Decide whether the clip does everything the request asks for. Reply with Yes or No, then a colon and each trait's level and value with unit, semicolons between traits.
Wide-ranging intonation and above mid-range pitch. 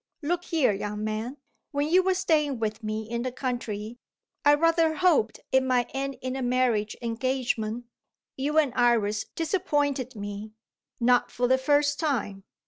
No: average, 4.8 semitones; very high, 255 Hz